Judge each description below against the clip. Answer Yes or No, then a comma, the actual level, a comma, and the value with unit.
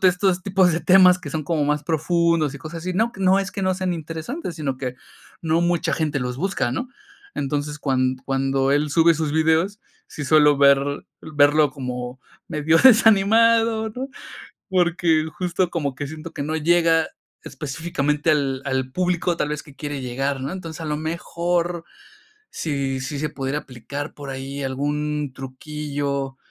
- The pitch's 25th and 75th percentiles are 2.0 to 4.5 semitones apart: Yes, average, 3.8 semitones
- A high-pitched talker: No, medium, 155 Hz